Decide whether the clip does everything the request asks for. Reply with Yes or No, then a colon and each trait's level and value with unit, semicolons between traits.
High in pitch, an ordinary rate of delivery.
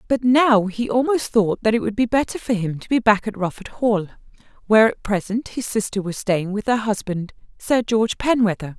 No: high, 220 Hz; fast, 210 wpm